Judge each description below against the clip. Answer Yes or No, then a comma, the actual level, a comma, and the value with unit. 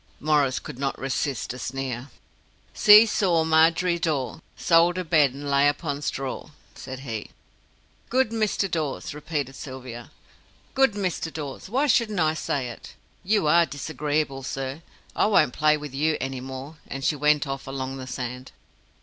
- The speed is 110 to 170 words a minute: Yes, average, 160 wpm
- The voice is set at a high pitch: No, medium, 145 Hz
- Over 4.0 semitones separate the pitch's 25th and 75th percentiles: No, average, 3.7 semitones